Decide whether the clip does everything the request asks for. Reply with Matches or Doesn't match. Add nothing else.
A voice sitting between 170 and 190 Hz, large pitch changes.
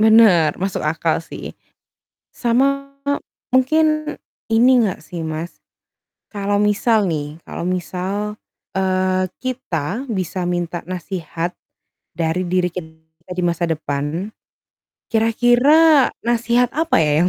Matches